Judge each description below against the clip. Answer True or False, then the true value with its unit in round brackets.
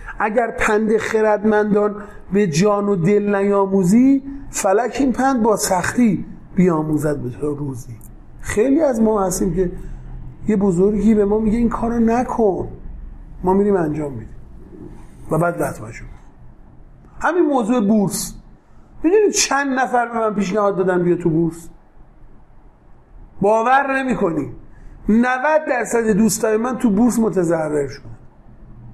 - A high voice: True (205 Hz)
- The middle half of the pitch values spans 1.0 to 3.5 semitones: False (5.0 semitones)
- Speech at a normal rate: True (125 wpm)